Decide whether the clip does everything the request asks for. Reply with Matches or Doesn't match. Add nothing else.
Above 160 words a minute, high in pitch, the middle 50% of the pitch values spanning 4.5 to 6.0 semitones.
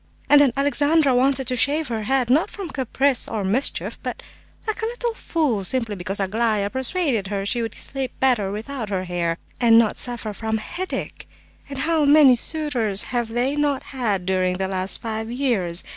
Matches